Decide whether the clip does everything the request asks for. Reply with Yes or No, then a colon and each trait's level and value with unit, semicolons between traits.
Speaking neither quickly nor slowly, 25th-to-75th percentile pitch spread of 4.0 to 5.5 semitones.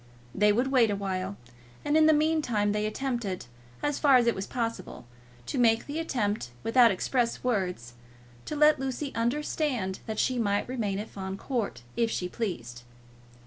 Yes: average, 165 wpm; average, 4.8 semitones